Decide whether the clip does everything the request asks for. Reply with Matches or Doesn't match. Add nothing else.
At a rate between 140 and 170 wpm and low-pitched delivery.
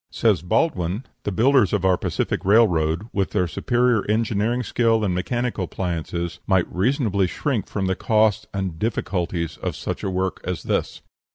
Matches